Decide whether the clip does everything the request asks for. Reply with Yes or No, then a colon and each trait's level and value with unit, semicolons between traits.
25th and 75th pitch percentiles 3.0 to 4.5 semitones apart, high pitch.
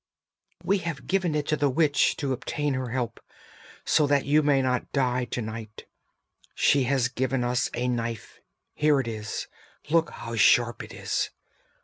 No: average, 3.3 semitones; low, 130 Hz